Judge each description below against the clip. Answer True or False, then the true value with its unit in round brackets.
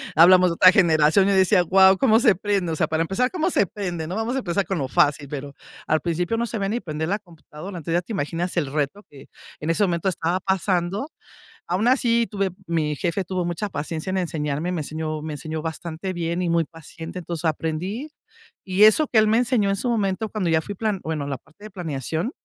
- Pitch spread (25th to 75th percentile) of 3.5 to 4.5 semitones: True (4.0 semitones)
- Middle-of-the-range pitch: True (175 Hz)